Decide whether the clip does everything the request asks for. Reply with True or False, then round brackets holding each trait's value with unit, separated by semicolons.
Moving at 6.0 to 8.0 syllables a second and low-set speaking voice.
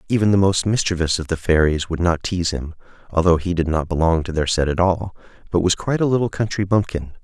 True (6.2 syllables/s; 90 Hz)